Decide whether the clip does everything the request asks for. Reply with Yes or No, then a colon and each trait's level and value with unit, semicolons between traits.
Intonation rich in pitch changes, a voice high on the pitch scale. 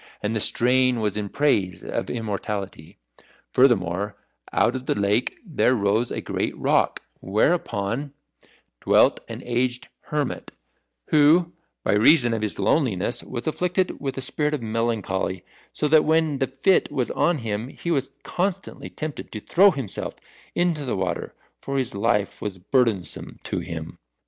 No: wide, 6.1 semitones; low, 120 Hz